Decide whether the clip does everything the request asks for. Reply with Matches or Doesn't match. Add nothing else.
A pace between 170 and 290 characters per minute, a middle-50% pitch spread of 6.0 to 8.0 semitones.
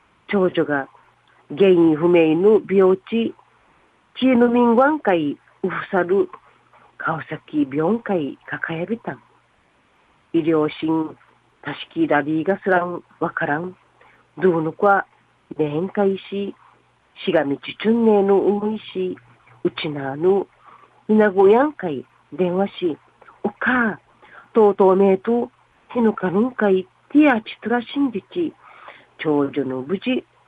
Doesn't match